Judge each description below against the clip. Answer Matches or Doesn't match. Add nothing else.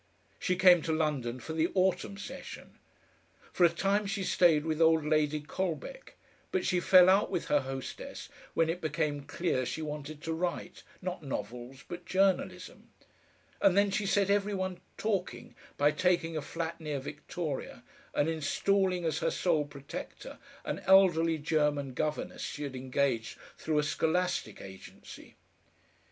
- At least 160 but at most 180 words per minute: Doesn't match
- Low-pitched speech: Doesn't match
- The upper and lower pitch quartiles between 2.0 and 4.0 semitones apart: Matches